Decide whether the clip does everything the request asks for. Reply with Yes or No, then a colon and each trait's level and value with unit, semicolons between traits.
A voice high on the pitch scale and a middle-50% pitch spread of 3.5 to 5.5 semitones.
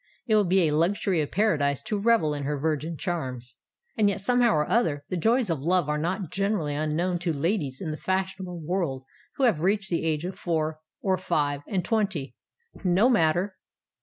No: medium, 175 Hz; average, 4.5 semitones